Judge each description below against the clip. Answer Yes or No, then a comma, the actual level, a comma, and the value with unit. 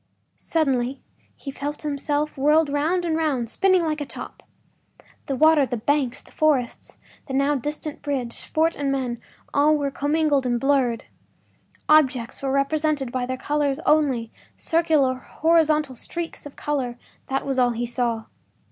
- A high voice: Yes, very high, 280 Hz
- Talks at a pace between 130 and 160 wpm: Yes, average, 150 wpm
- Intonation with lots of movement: No, average, 3.0 semitones